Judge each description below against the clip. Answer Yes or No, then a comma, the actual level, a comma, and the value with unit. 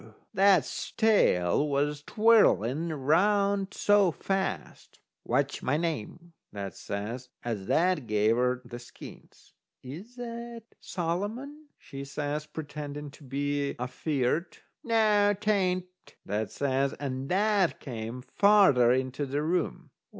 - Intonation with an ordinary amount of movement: No, wide, 7.4 semitones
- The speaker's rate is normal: No, slow, 115 wpm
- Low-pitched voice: No, medium, 150 Hz